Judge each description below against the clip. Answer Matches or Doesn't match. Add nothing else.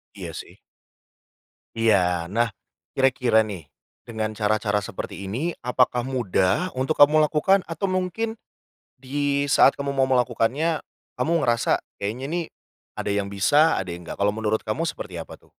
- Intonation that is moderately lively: Doesn't match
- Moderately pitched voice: Doesn't match